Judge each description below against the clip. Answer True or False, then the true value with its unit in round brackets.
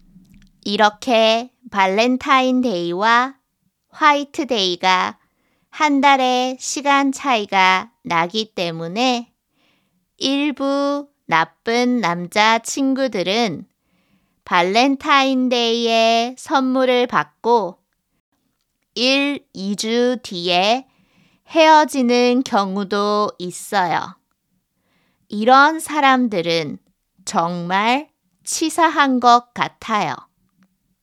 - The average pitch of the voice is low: False (235 Hz)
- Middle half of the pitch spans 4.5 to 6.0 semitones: True (5.6 semitones)